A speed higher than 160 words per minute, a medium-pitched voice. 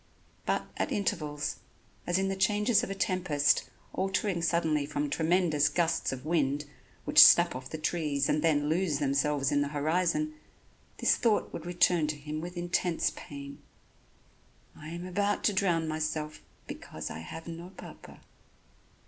No: average, 155 wpm; medium, 165 Hz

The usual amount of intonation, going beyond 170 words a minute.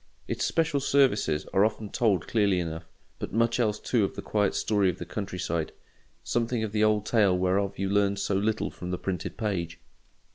Yes: average, 3.2 semitones; average, 195 wpm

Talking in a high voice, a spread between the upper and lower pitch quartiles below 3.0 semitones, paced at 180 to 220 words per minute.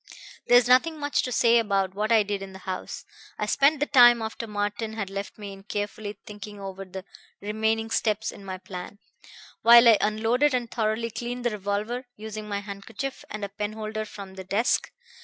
Yes: high, 215 Hz; narrow, 2.6 semitones; average, 190 wpm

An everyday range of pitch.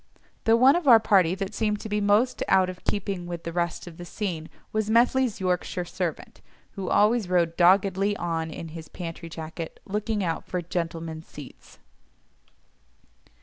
Yes: average, 3.8 semitones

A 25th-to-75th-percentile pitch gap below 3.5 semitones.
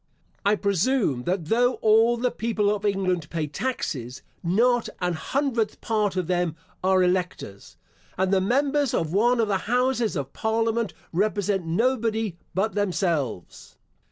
No: average, 4.5 semitones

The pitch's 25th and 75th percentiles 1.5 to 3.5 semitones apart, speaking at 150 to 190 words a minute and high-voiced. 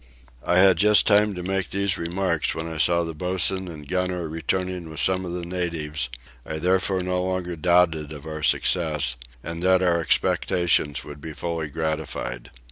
No: average, 2.7 semitones; average, 175 wpm; very low, 85 Hz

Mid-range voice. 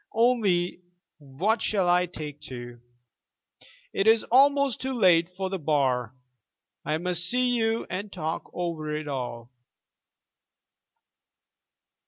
Yes: medium, 180 Hz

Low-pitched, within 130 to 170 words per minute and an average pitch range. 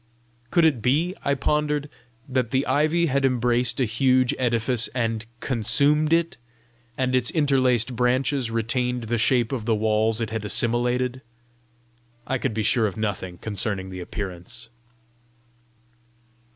Yes: low, 125 Hz; average, 140 wpm; average, 3.2 semitones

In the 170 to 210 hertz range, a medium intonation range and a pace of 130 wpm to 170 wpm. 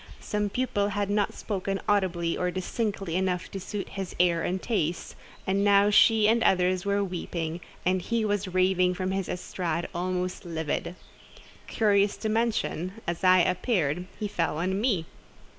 No: medium, 185 Hz; narrow, 2.3 semitones; average, 160 wpm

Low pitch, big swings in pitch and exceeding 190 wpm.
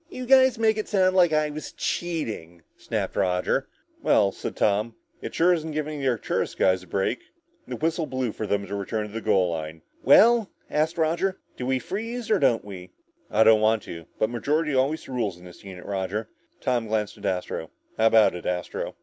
Yes: low, 115 Hz; wide, 8.2 semitones; average, 200 wpm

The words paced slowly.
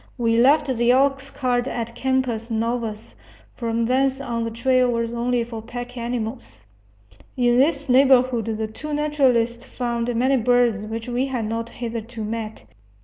No: average, 145 wpm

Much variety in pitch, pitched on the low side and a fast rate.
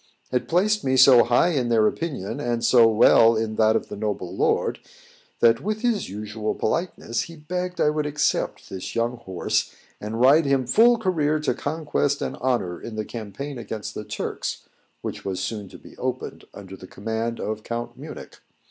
No: wide, 5.7 semitones; low, 120 Hz; average, 185 wpm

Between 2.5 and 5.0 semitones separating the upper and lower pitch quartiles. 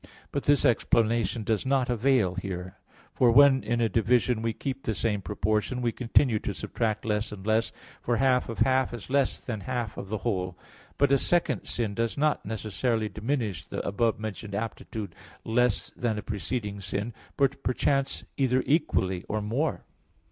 Yes: average, 3.5 semitones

